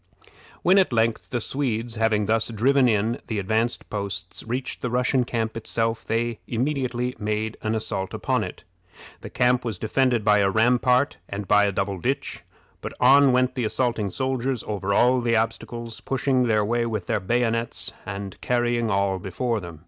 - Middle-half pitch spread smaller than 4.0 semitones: Yes, average, 2.8 semitones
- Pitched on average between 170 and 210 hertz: No, low, 115 Hz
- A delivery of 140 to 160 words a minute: No, average, 170 wpm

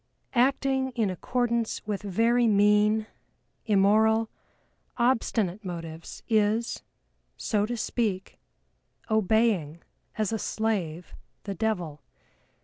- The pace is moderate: No, slow, 90 wpm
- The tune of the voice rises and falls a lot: No, average, 3.0 semitones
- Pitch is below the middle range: No, high, 215 Hz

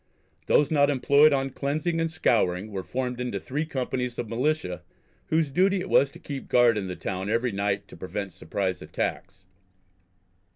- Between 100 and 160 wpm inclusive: No, average, 170 wpm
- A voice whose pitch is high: No, low, 125 Hz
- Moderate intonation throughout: No, wide, 6.4 semitones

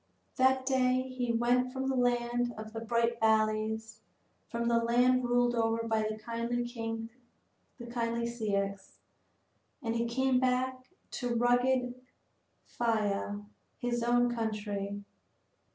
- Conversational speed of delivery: No, slow, 115 wpm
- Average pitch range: No, narrow, 1.7 semitones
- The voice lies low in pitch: No, high, 235 Hz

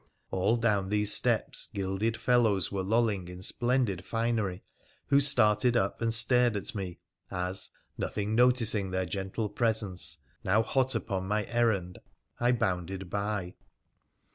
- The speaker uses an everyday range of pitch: Yes, average, 3.6 semitones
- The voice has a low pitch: Yes, low, 105 Hz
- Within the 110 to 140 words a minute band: Yes, slow, 135 wpm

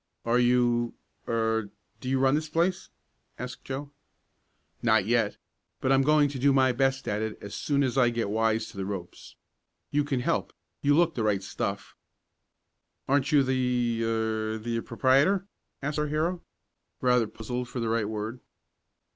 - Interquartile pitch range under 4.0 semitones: Yes, average, 3.6 semitones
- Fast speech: No, average, 165 wpm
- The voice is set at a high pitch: No, low, 125 Hz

